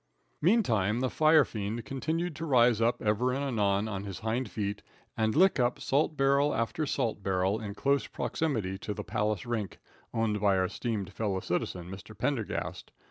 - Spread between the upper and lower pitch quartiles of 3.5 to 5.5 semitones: Yes, average, 5.2 semitones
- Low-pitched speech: Yes, low, 110 Hz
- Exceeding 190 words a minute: No, average, 170 wpm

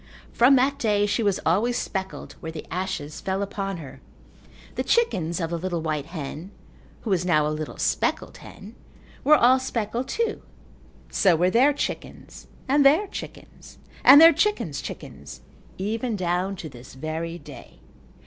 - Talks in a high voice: Yes, high, 195 Hz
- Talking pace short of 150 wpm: No, average, 160 wpm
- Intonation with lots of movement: Yes, wide, 6.7 semitones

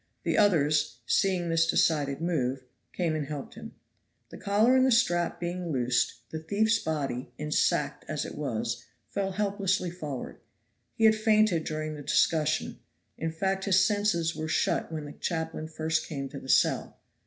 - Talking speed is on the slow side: No, average, 165 wpm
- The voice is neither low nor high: Yes, medium, 160 Hz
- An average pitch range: Yes, average, 4.5 semitones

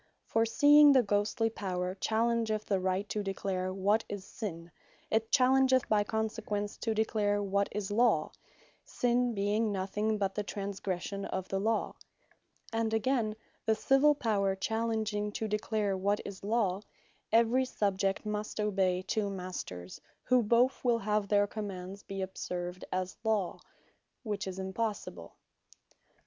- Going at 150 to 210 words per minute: No, average, 140 wpm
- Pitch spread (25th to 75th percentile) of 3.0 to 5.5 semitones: No, narrow, 2.5 semitones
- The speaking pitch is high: Yes, high, 210 Hz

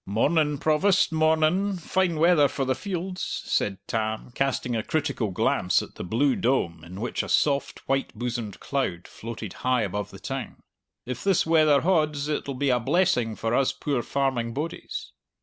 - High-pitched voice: No, medium, 140 Hz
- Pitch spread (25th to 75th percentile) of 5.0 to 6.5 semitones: Yes, average, 5.3 semitones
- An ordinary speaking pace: Yes, average, 165 wpm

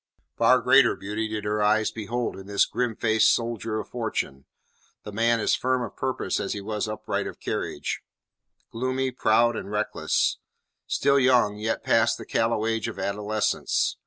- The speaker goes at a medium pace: Yes, average, 160 wpm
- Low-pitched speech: Yes, low, 110 Hz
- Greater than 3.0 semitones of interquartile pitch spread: No, narrow, 2.4 semitones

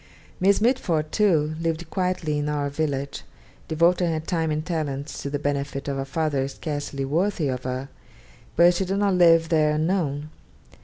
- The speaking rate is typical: Yes, average, 165 wpm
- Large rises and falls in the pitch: No, average, 3.4 semitones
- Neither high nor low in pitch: Yes, medium, 155 Hz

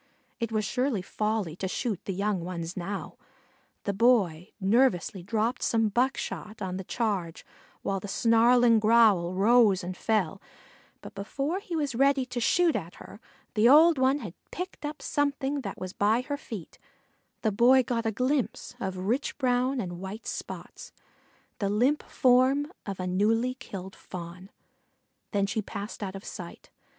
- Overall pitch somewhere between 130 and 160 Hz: No, high, 220 Hz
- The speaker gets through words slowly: No, average, 160 wpm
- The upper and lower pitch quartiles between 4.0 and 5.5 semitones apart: Yes, average, 4.8 semitones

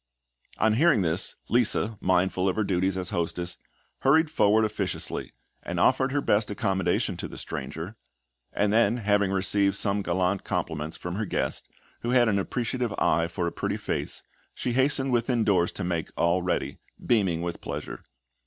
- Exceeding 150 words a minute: Yes, average, 165 wpm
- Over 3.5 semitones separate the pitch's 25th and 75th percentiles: Yes, average, 4.2 semitones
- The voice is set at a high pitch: No, low, 100 Hz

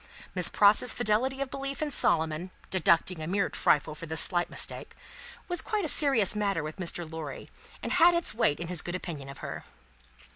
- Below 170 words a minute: No, average, 190 wpm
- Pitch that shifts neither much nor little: No, wide, 8.4 semitones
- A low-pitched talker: No, high, 190 Hz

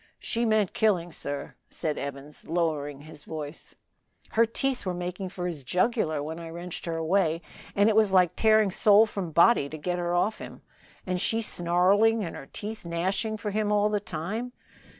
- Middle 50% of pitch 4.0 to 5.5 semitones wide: Yes, average, 4.6 semitones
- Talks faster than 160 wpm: Yes, average, 185 wpm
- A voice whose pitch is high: No, medium, 180 Hz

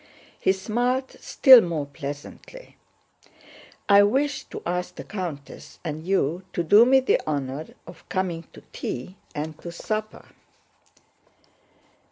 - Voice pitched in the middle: Yes, medium, 180 Hz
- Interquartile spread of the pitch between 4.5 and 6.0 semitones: Yes, wide, 5.5 semitones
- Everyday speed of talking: No, slow, 125 wpm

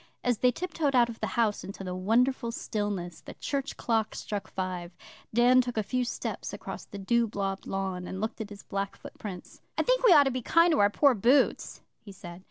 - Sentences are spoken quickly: Yes, fast, 215 wpm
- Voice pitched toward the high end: Yes, high, 220 Hz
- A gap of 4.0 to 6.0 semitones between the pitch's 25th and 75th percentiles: Yes, average, 4.5 semitones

